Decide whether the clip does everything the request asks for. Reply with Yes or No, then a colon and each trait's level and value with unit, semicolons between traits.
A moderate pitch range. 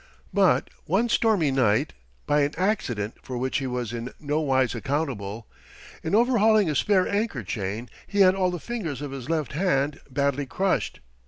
No: wide, 7.0 semitones